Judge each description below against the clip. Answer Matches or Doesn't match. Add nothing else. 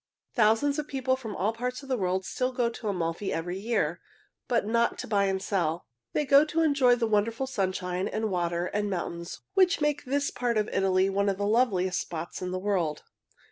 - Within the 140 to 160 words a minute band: Doesn't match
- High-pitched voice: Matches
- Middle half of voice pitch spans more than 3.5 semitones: Matches